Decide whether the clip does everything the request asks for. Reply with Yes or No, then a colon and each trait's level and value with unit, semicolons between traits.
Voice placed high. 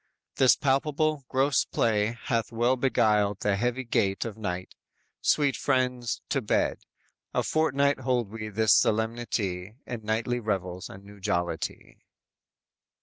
No: low, 115 Hz